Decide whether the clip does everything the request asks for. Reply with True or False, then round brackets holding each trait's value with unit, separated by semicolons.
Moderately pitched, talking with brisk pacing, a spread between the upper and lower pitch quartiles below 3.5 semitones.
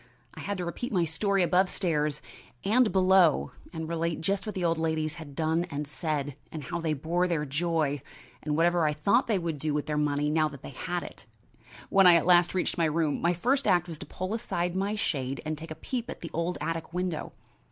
True (165 Hz; 225 wpm; 2.8 semitones)